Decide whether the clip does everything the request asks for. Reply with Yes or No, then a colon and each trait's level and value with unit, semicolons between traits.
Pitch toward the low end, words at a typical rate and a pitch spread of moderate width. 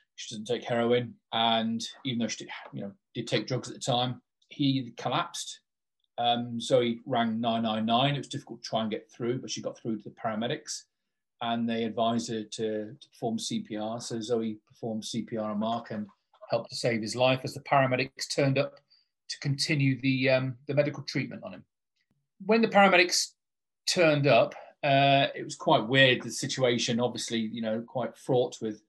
Yes: low, 120 Hz; average, 185 wpm; average, 3.5 semitones